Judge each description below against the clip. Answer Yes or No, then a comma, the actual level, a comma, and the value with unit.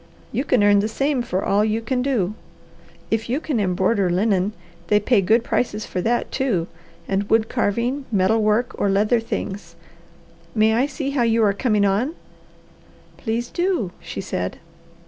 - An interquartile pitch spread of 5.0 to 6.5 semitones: No, average, 3.4 semitones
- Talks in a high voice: Yes, high, 220 Hz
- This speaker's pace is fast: No, average, 165 wpm